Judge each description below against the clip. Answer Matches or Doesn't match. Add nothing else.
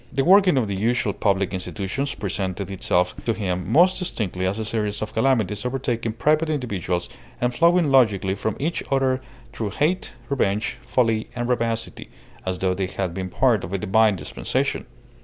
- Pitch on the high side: Doesn't match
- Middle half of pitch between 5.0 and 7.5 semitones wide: Matches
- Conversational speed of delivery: Matches